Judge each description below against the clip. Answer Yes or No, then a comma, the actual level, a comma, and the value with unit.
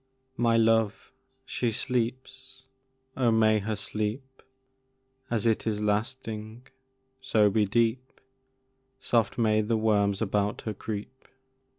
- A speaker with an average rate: No, slow, 110 wpm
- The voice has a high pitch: No, low, 110 Hz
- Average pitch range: No, narrow, 2.2 semitones